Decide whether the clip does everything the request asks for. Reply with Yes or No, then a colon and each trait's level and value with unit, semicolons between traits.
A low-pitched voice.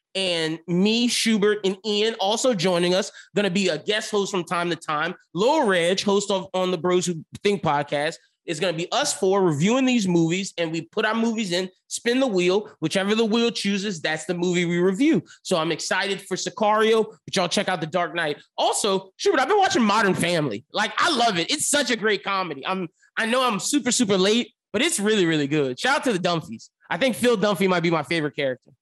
No: high, 190 Hz